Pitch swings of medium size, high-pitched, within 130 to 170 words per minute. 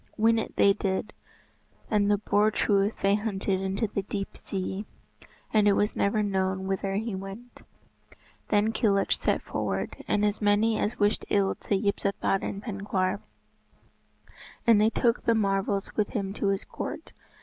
No: narrow, 1.5 semitones; high, 205 Hz; average, 155 wpm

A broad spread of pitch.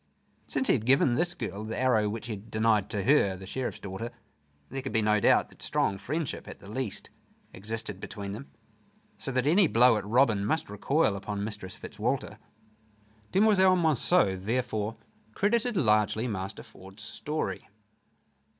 No: average, 4.9 semitones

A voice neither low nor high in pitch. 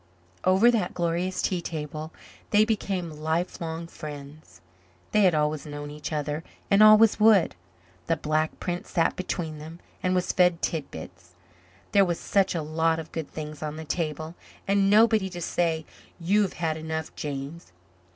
Yes: medium, 165 Hz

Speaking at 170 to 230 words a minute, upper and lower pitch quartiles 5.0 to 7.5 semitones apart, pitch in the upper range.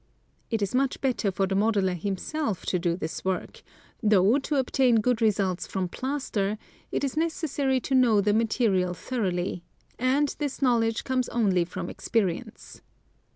No: average, 155 wpm; average, 5.3 semitones; high, 220 Hz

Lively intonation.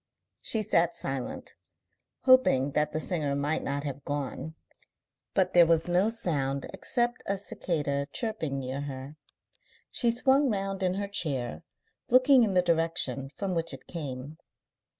Yes: wide, 6.0 semitones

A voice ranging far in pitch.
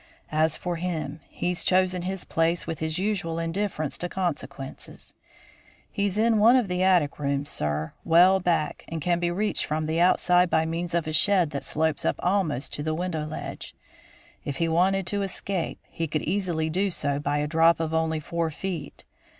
No: average, 2.8 semitones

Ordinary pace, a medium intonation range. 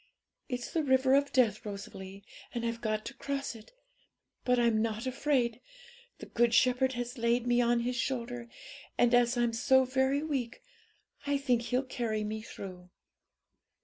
No: average, 160 wpm; narrow, 2.3 semitones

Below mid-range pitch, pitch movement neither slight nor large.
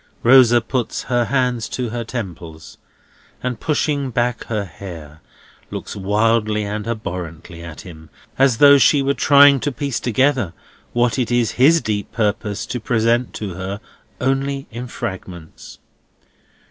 Yes: low, 115 Hz; average, 4.1 semitones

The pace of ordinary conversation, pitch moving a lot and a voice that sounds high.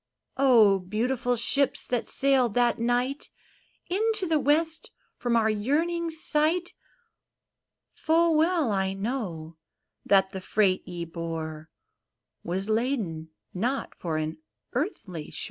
No: slow, 115 wpm; wide, 7.6 semitones; high, 240 Hz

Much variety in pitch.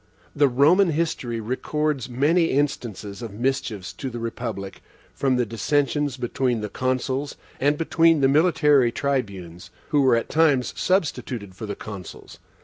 No: average, 4.3 semitones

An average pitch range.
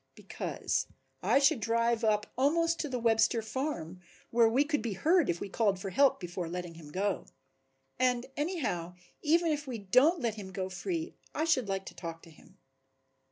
No: wide, 7.3 semitones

